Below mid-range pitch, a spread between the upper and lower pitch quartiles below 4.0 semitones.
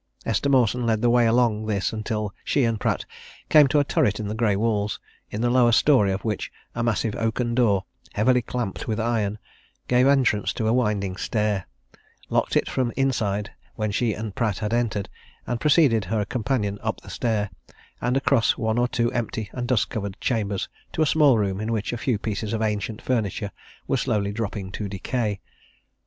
Yes: low, 110 Hz; average, 2.8 semitones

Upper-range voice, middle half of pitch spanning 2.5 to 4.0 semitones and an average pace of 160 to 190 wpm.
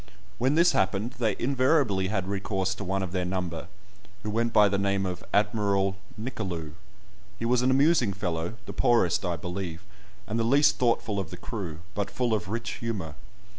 No: low, 100 Hz; average, 3.7 semitones; average, 180 wpm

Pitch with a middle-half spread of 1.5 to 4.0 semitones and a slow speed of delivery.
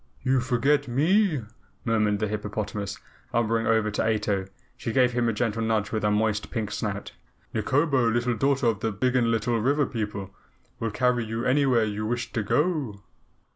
No: average, 3.1 semitones; average, 165 wpm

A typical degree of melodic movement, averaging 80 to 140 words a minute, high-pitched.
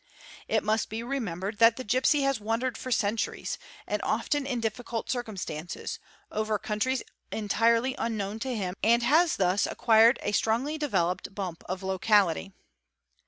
Yes: average, 3.7 semitones; slow, 135 wpm; high, 225 Hz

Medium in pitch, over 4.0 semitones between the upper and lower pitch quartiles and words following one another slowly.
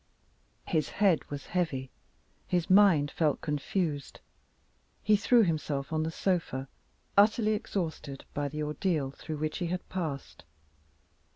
Yes: medium, 160 Hz; average, 4.4 semitones; slow, 125 wpm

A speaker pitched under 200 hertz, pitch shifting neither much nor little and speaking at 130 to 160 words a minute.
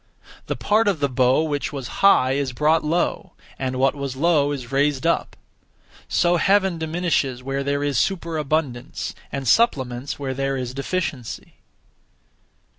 Yes: medium, 140 Hz; average, 3.7 semitones; average, 145 wpm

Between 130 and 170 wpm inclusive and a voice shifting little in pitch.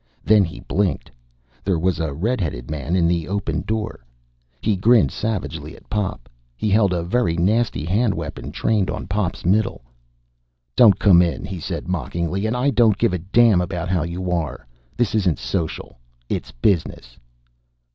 No: average, 165 wpm; average, 4.0 semitones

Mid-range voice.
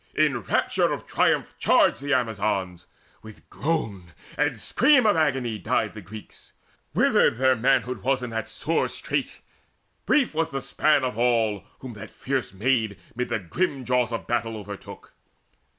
No: low, 120 Hz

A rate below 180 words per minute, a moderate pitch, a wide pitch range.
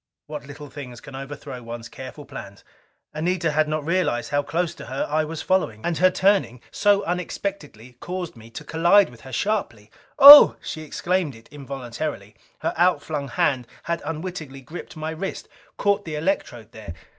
Yes: average, 170 wpm; medium, 150 Hz; wide, 5.7 semitones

